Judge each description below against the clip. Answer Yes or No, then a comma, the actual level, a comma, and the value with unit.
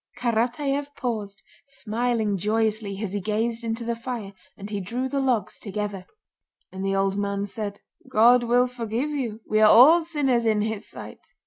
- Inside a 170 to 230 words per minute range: Yes, average, 175 wpm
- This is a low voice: No, high, 225 Hz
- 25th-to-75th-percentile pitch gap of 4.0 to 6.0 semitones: No, average, 3.2 semitones